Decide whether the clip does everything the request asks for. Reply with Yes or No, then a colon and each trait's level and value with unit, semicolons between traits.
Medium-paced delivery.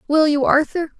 Yes: average, 180 wpm